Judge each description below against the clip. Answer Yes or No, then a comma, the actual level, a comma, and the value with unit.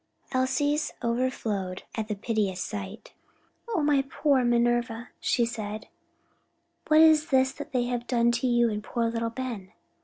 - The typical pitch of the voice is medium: No, high, 240 Hz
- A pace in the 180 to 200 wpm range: No, average, 145 wpm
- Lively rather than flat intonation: No, average, 3.0 semitones